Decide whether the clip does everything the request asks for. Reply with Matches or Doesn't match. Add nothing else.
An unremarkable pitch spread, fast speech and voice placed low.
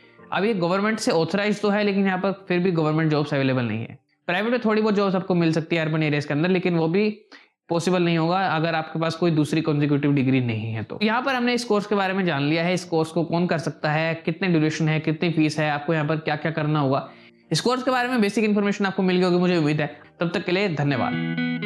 Doesn't match